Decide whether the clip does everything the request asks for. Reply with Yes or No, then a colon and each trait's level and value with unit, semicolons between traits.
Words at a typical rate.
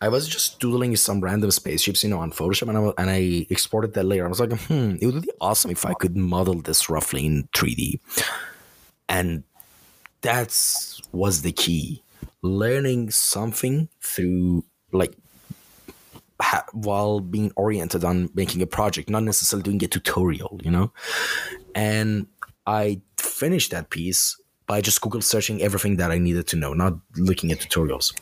Yes: average, 165 wpm